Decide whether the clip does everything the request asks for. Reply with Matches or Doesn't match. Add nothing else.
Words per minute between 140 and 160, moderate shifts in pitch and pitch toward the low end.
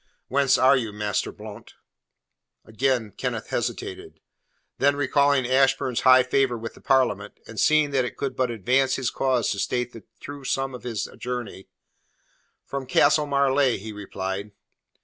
Matches